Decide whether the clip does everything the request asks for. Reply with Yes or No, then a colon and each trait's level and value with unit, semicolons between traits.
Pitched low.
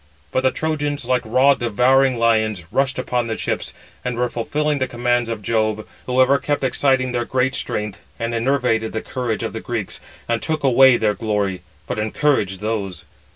Yes: low, 120 Hz